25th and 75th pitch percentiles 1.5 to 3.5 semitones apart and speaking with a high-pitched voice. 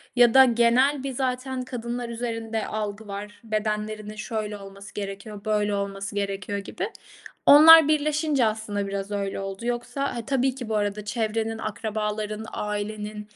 Yes: average, 2.9 semitones; high, 215 Hz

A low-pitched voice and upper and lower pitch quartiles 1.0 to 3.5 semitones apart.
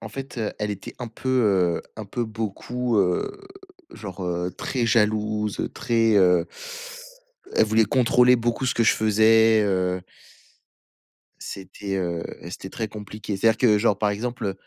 Yes: low, 110 Hz; average, 2.9 semitones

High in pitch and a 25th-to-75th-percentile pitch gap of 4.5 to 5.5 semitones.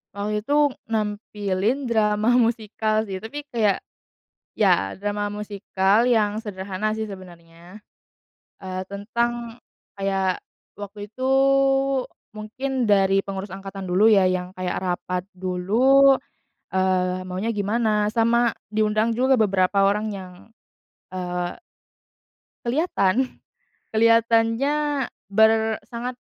No: high, 210 Hz; average, 3.1 semitones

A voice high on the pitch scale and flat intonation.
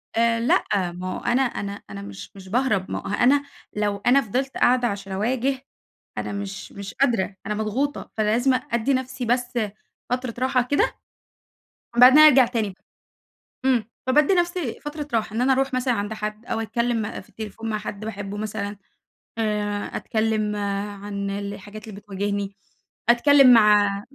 No: high, 225 Hz; average, 3.8 semitones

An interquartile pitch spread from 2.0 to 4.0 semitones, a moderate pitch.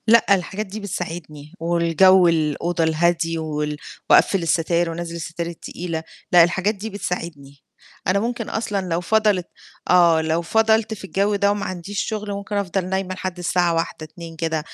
Yes: average, 3.2 semitones; medium, 175 Hz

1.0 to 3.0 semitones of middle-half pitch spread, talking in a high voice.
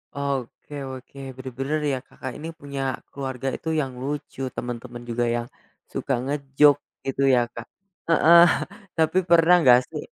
No: narrow, 2.5 semitones; low, 135 Hz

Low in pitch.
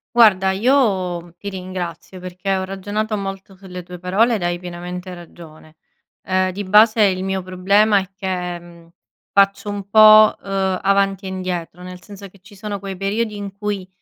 No: high, 190 Hz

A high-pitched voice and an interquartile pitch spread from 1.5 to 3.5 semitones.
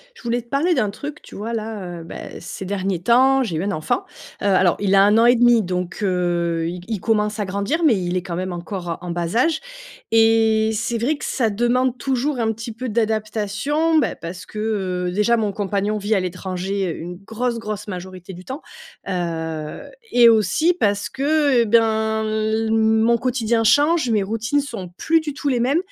No: high, 220 Hz; average, 4.1 semitones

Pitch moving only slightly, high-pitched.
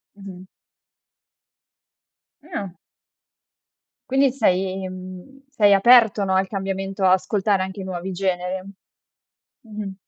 Yes: narrow, 1.9 semitones; high, 195 Hz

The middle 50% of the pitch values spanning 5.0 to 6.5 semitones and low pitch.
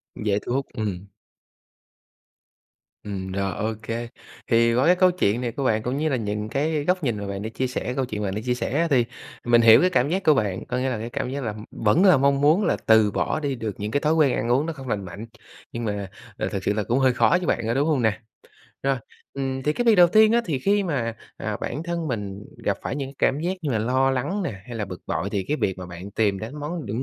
Yes: wide, 5.6 semitones; low, 125 Hz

